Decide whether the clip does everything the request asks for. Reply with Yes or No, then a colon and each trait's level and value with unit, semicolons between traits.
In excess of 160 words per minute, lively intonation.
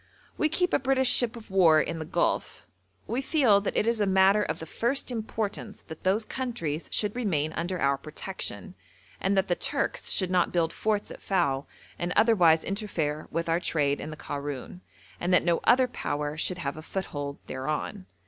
Yes: average, 190 wpm; wide, 5.7 semitones